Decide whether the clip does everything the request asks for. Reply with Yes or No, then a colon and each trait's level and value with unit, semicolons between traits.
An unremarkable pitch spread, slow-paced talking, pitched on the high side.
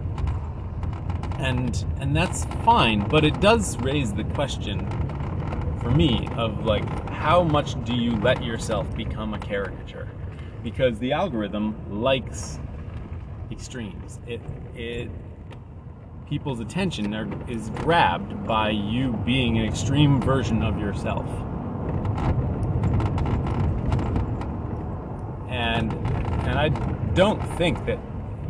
No: average, 3.4 semitones; slow, 105 wpm; low, 110 Hz